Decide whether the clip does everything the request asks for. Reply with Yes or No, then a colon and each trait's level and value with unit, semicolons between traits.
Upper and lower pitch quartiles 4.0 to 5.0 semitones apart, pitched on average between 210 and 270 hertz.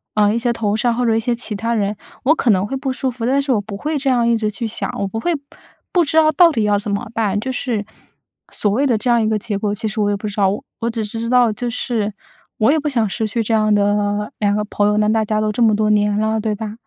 No: narrow, 2.6 semitones; high, 220 Hz